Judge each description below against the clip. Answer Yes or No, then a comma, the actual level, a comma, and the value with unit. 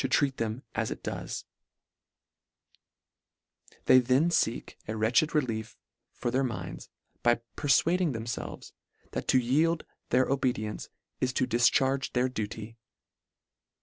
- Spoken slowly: Yes, slow, 100 wpm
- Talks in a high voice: No, low, 125 Hz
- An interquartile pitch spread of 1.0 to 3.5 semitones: Yes, average, 3.1 semitones